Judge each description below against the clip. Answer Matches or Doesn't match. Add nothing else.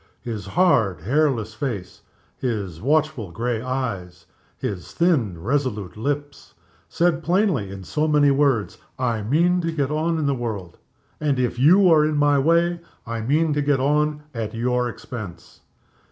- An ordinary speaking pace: Matches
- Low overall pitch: Matches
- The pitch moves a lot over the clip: Matches